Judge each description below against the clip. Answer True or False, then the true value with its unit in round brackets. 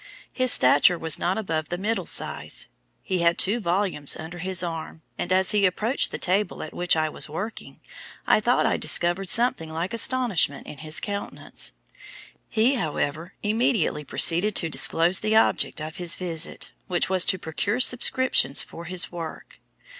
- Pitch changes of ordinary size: True (4.2 semitones)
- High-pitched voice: False (180 Hz)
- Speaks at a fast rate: False (165 wpm)